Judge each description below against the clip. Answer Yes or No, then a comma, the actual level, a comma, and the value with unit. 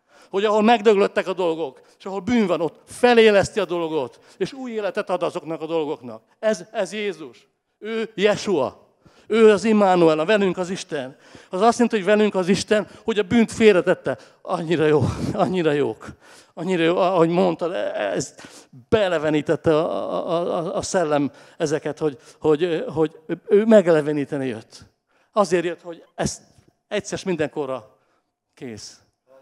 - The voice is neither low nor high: Yes, medium, 180 Hz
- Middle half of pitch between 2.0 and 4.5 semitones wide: No, average, 5.3 semitones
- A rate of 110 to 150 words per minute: Yes, average, 145 wpm